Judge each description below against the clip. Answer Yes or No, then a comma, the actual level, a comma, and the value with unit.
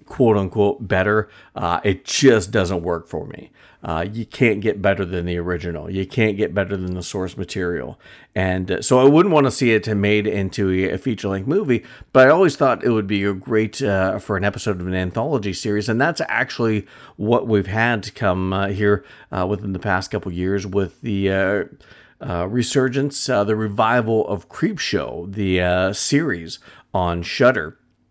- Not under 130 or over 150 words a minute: No, average, 190 wpm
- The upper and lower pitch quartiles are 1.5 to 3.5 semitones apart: Yes, average, 3.0 semitones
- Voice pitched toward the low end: Yes, low, 100 Hz